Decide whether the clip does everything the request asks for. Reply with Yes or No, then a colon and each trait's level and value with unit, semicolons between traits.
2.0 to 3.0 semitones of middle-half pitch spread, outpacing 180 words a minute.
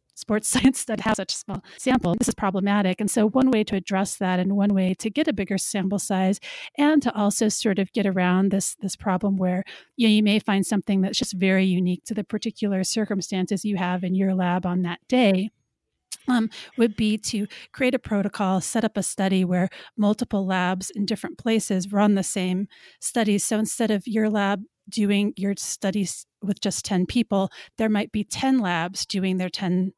Yes: narrow, 2.4 semitones; average, 200 wpm